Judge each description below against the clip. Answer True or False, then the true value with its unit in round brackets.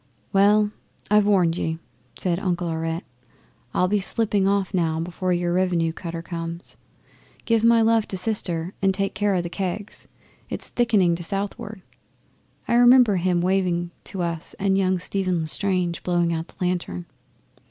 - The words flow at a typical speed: True (155 wpm)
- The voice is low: False (185 Hz)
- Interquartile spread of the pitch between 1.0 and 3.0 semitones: True (2.7 semitones)